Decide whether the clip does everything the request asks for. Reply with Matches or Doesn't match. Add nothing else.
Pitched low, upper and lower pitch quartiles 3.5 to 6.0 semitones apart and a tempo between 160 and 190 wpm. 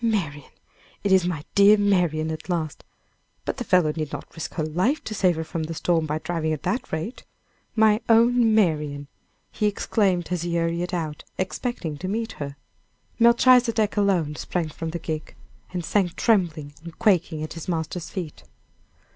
Doesn't match